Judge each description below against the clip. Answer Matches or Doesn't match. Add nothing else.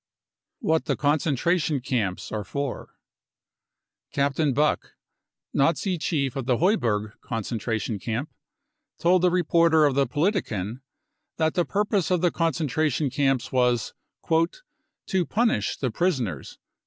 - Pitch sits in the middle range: Matches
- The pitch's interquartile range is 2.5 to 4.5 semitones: Doesn't match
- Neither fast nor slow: Doesn't match